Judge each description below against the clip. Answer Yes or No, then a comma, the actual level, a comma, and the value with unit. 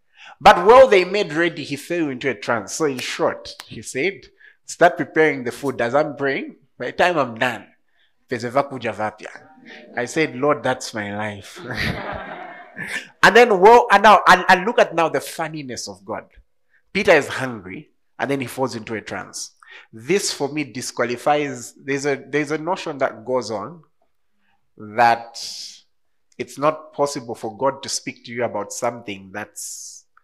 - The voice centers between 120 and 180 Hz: Yes, low, 135 Hz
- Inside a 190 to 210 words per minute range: No, average, 165 wpm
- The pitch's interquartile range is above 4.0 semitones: Yes, average, 4.7 semitones